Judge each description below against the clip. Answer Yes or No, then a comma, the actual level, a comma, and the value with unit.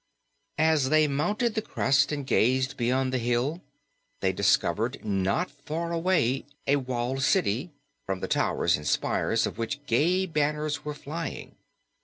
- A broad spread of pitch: No, average, 3.9 semitones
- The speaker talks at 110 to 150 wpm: Yes, average, 145 wpm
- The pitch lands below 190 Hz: Yes, medium, 140 Hz